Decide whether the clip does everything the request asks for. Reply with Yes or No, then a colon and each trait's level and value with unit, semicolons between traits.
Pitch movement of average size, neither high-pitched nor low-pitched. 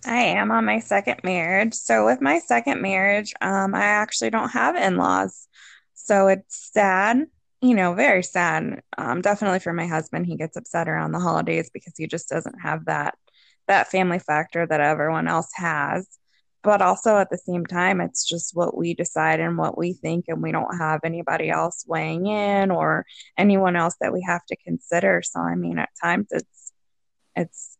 Yes: average, 3.5 semitones; medium, 180 Hz